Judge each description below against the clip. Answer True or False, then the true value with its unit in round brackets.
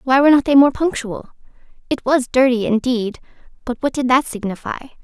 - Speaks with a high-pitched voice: True (255 Hz)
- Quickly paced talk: False (180 wpm)